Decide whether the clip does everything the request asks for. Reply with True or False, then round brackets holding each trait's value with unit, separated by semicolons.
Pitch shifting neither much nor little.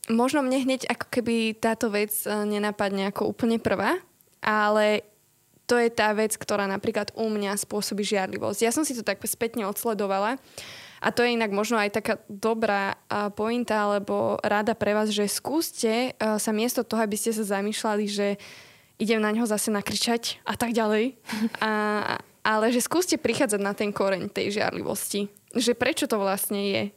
False (2.0 semitones)